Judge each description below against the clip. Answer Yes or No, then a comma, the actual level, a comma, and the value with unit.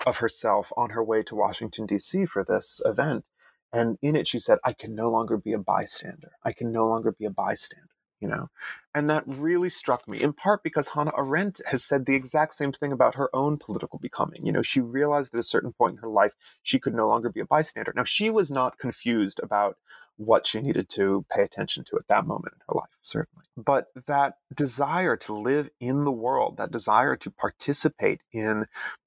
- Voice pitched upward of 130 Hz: Yes, medium, 140 Hz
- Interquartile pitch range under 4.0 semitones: No, average, 4.9 semitones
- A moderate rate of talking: No, fast, 215 wpm